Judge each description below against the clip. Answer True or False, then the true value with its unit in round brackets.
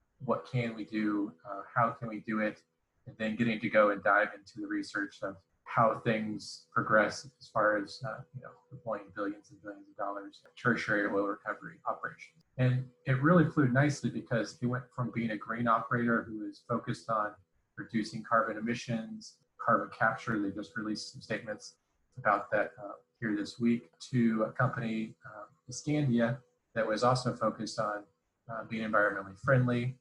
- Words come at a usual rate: True (175 wpm)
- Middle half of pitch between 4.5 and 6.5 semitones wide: False (3.0 semitones)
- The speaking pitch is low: True (115 Hz)